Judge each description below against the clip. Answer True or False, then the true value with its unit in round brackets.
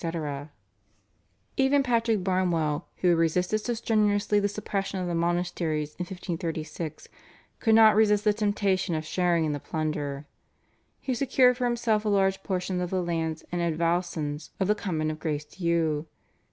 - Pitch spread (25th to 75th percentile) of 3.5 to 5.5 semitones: True (4.4 semitones)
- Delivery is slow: False (155 wpm)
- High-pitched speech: False (180 Hz)